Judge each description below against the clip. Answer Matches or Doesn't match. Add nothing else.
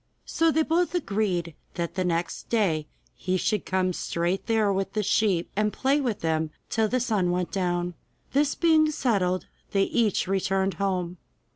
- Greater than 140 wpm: Matches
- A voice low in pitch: Doesn't match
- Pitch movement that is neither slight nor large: Matches